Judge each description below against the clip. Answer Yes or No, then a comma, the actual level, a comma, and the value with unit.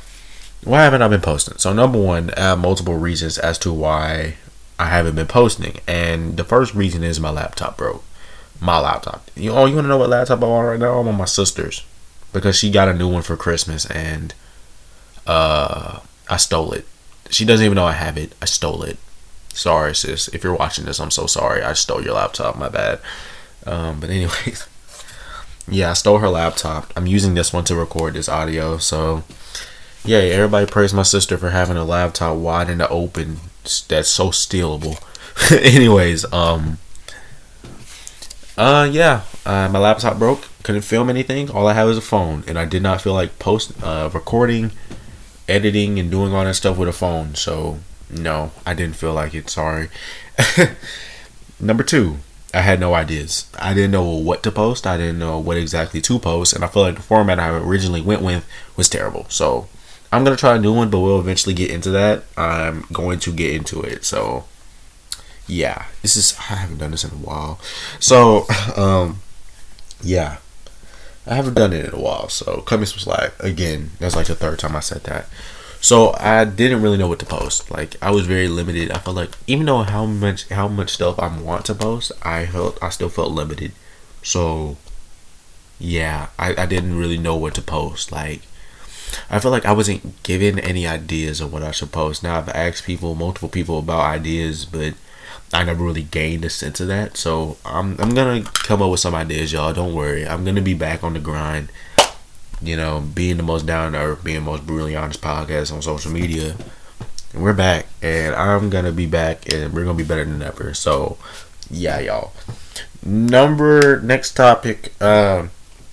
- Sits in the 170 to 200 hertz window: No, very low, 85 Hz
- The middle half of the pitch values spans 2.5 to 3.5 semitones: No, average, 4.0 semitones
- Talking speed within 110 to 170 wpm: No, average, 195 wpm